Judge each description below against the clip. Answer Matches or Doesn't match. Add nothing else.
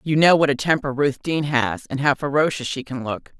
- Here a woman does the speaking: Matches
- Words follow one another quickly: Matches